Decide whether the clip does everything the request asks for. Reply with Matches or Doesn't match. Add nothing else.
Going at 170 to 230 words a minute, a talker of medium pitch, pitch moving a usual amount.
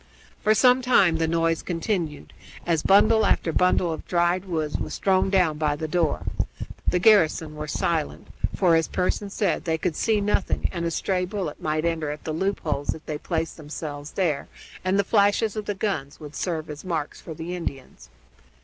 Matches